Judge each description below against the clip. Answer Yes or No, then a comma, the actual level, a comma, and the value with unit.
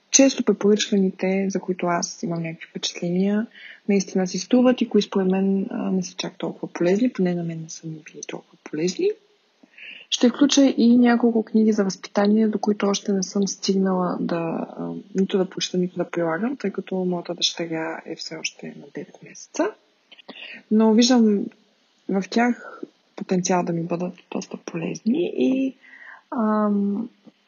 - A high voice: Yes, high, 200 Hz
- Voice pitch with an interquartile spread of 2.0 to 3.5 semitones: No, average, 4.2 semitones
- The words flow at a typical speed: Yes, average, 155 wpm